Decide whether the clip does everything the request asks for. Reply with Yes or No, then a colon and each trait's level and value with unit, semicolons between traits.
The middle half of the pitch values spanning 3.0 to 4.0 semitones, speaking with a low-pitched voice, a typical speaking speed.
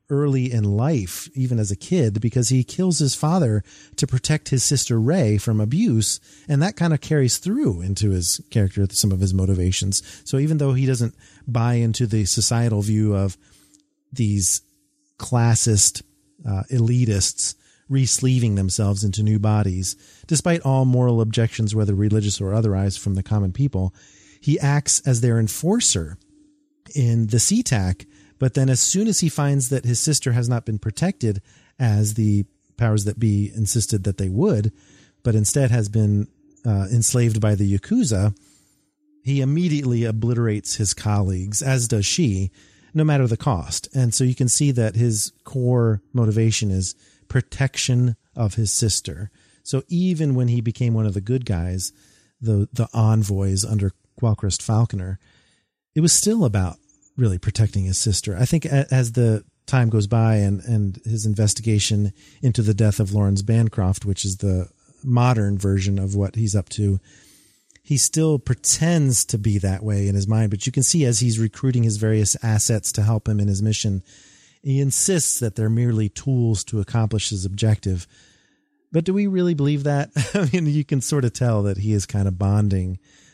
No: average, 4.6 semitones; low, 110 Hz; average, 170 wpm